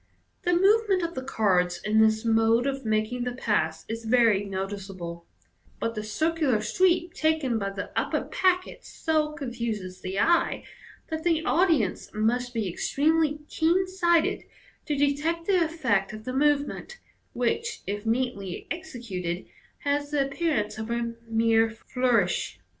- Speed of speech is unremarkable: Yes, average, 145 wpm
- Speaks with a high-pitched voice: Yes, high, 245 Hz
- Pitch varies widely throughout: Yes, wide, 6.8 semitones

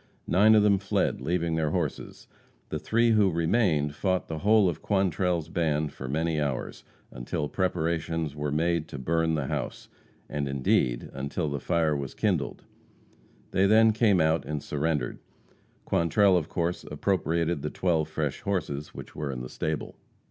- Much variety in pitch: No, average, 3.7 semitones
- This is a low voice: Yes, very low, 80 Hz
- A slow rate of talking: No, average, 165 wpm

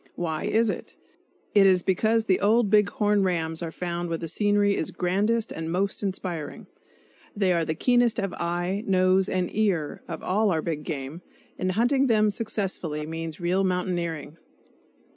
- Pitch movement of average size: Yes, average, 3.6 semitones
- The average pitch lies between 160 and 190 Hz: Yes, medium, 185 Hz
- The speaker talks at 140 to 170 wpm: Yes, average, 165 wpm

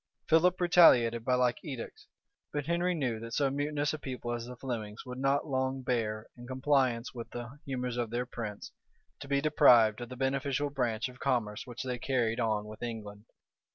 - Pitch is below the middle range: Yes, low, 125 Hz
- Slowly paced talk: No, average, 190 wpm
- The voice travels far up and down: No, average, 2.9 semitones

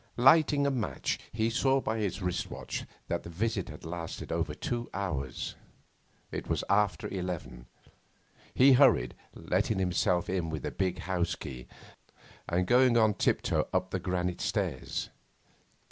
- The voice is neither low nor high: No, very low, 95 Hz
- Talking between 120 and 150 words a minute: Yes, average, 145 wpm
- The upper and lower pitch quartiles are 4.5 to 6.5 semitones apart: Yes, average, 5.1 semitones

